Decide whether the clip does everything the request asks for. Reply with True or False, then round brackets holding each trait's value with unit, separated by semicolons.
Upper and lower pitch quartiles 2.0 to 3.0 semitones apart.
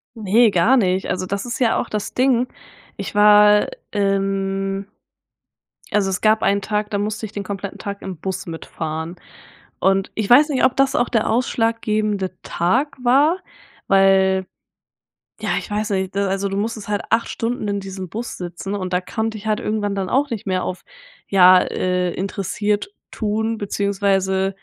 True (2.4 semitones)